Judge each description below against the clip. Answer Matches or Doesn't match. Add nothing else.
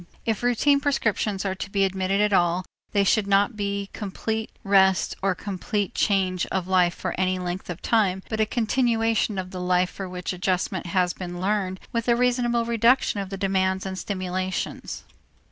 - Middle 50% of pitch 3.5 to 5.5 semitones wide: Doesn't match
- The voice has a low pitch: Doesn't match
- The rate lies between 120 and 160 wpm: Doesn't match